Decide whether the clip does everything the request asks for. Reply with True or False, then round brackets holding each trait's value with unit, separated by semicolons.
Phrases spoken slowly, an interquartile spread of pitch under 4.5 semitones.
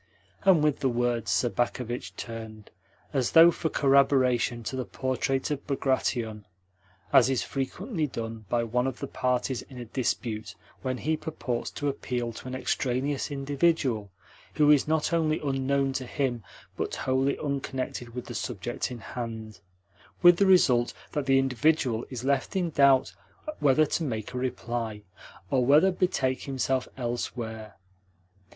False (150 wpm; 2.8 semitones)